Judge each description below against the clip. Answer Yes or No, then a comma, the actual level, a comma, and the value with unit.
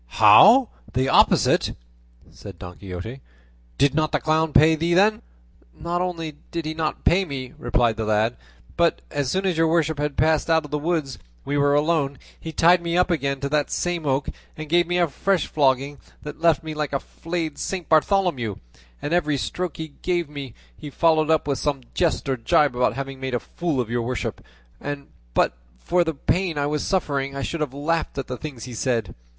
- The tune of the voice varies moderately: Yes, average, 3.7 semitones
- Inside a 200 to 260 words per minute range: Yes, fast, 205 wpm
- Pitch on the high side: No, medium, 150 Hz